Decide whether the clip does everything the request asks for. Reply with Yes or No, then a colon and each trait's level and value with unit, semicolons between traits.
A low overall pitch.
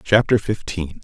Yes: low, 100 Hz